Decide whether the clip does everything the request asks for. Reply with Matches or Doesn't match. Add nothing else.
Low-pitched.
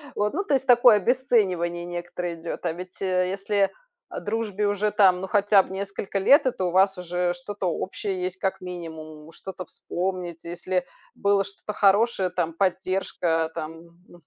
Doesn't match